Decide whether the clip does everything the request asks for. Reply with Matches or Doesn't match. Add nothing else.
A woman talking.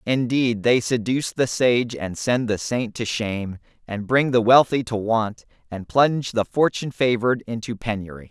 Doesn't match